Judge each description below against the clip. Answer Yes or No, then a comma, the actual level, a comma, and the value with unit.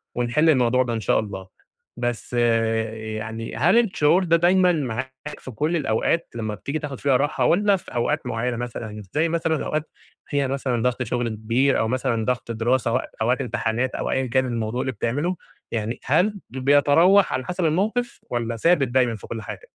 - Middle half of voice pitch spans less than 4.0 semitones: No, average, 4.8 semitones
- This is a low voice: Yes, low, 125 Hz